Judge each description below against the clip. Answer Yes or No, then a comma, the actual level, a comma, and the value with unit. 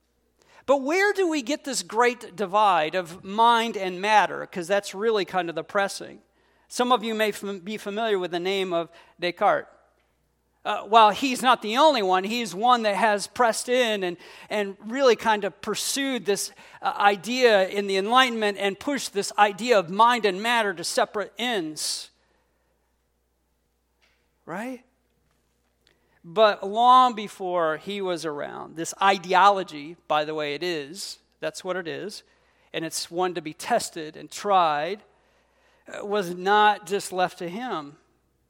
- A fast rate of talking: No, average, 155 wpm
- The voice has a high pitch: Yes, high, 200 Hz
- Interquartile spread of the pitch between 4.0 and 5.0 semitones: Yes, average, 4.7 semitones